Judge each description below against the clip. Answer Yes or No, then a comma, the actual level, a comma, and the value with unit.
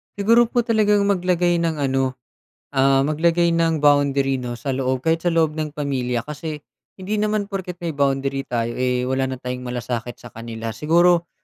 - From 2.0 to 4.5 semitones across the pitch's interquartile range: No, average, 5.1 semitones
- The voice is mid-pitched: Yes, medium, 145 Hz